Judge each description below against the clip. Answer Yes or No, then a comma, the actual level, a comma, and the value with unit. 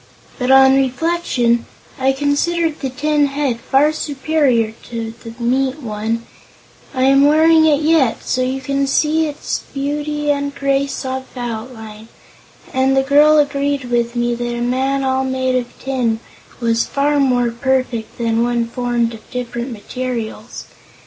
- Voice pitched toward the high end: Yes, very high, 265 Hz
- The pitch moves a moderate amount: Yes, average, 3.0 semitones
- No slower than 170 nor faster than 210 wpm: No, average, 150 wpm